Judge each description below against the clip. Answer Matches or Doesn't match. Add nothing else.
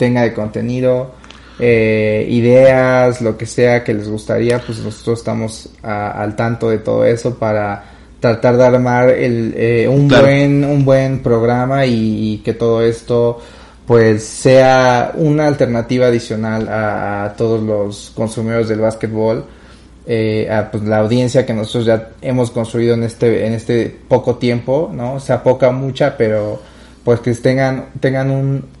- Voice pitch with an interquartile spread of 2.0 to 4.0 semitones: Matches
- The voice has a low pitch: Matches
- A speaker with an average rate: Matches